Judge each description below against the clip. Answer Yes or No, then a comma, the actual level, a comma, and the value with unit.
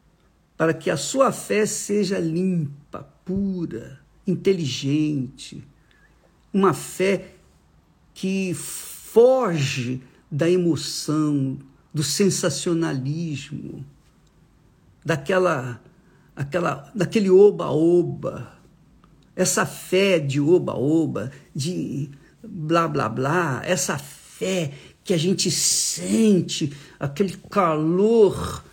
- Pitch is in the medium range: Yes, medium, 170 Hz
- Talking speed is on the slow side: Yes, slow, 80 wpm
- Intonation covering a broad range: No, average, 4.5 semitones